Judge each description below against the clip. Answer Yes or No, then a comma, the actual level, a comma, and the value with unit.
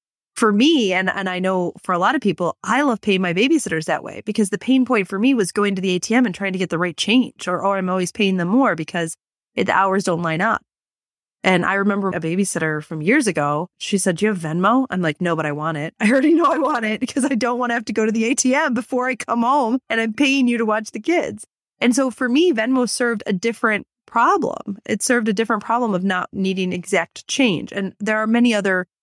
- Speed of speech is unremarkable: No, fast, 255 wpm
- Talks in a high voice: Yes, high, 215 Hz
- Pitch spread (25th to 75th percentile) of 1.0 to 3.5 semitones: No, average, 5.0 semitones